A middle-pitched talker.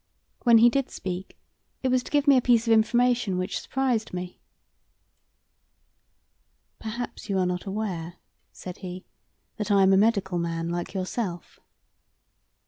No: high, 200 Hz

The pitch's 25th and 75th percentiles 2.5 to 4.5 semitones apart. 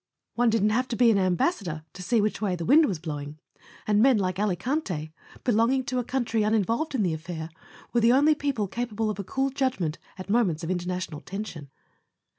No: average, 5.3 semitones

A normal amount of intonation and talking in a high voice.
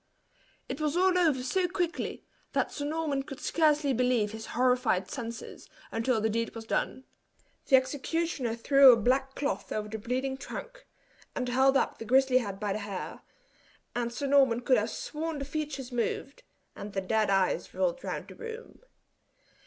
Yes: average, 4.5 semitones; very high, 260 Hz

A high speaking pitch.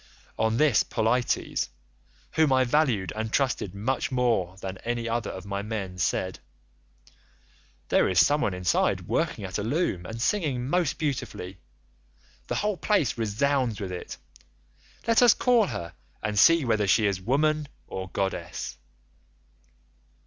No: low, 115 Hz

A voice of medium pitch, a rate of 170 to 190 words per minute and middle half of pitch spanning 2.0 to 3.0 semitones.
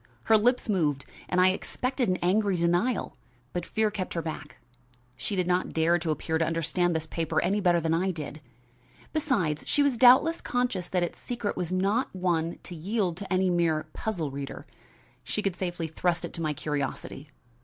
No: medium, 180 Hz; average, 185 wpm; average, 4.0 semitones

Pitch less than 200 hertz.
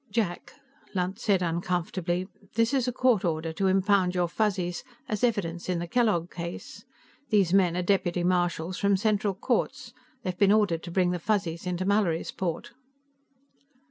Yes: medium, 185 Hz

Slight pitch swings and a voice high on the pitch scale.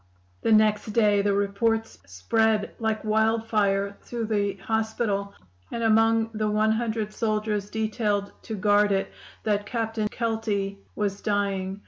Yes: narrow, 1.7 semitones; high, 215 Hz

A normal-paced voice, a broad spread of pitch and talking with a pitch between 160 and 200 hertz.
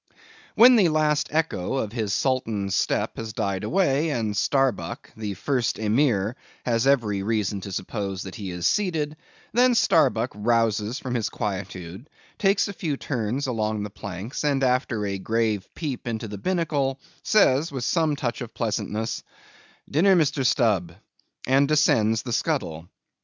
No: average, 150 wpm; wide, 5.8 semitones; low, 120 Hz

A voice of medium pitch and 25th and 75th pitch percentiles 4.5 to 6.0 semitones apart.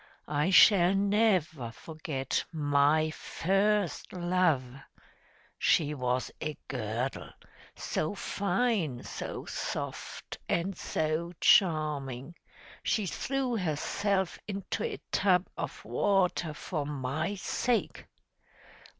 Yes: medium, 170 Hz; average, 5.1 semitones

